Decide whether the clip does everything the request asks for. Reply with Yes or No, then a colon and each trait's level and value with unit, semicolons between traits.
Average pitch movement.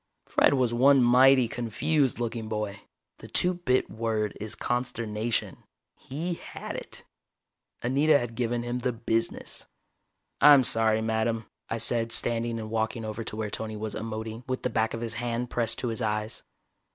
No: narrow, 2.1 semitones